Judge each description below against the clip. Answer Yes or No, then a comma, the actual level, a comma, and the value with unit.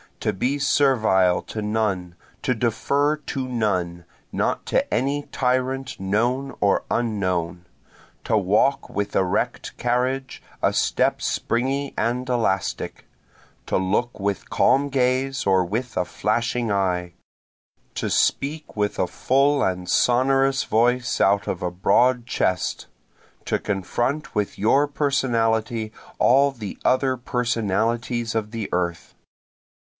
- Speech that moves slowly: Yes, slow, 120 wpm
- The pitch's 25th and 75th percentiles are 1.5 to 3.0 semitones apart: No, average, 4.8 semitones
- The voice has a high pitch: No, low, 115 Hz